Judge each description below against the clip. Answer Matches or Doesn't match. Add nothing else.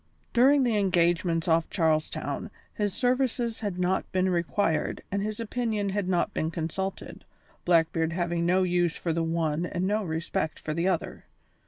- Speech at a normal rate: Matches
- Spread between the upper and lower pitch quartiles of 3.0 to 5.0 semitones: Matches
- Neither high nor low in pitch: Matches